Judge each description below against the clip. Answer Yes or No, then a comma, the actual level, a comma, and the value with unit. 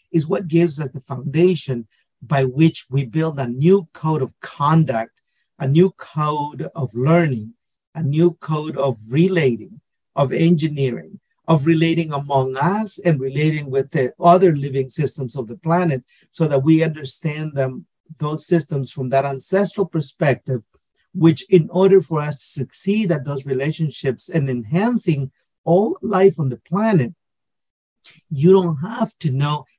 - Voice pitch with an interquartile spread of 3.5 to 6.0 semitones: Yes, average, 4.0 semitones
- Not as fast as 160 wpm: Yes, average, 150 wpm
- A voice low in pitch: No, medium, 155 Hz